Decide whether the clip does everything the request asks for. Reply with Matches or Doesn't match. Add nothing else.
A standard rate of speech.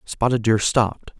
Matches